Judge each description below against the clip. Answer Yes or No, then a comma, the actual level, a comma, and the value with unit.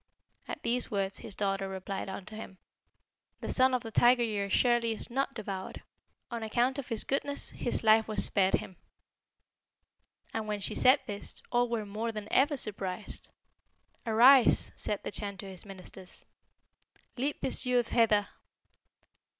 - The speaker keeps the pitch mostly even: No, average, 3.4 semitones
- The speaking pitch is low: No, high, 220 Hz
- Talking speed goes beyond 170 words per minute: No, average, 155 wpm